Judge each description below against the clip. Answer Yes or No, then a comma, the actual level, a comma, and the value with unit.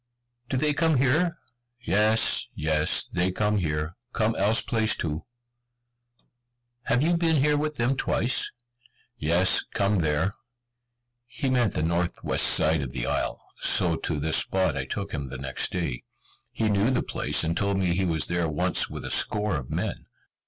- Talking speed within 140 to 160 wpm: No, average, 170 wpm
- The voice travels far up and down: Yes, wide, 7.2 semitones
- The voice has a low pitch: Yes, very low, 95 Hz